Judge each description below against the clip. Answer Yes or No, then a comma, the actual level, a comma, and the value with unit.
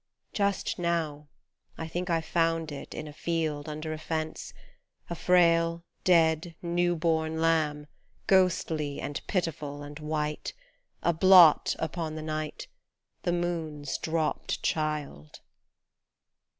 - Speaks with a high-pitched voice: No, medium, 160 Hz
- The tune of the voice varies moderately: No, narrow, 2.0 semitones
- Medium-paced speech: No, slow, 120 wpm